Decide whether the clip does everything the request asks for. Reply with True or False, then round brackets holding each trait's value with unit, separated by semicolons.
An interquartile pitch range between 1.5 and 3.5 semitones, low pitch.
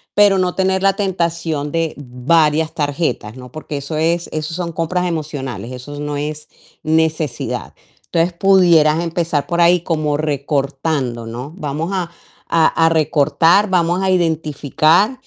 False (2.9 semitones; 160 Hz)